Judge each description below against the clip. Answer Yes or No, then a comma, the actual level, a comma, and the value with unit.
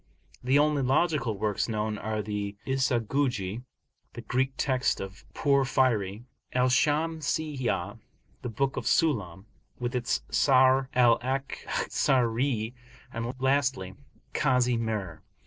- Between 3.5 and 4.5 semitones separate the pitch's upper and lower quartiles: Yes, average, 3.8 semitones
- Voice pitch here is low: Yes, low, 125 Hz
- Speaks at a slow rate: Yes, slow, 110 wpm